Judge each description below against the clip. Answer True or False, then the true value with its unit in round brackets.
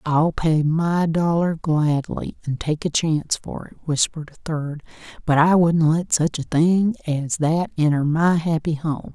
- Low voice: False (160 Hz)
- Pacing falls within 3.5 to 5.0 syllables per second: True (4.2 syllables/s)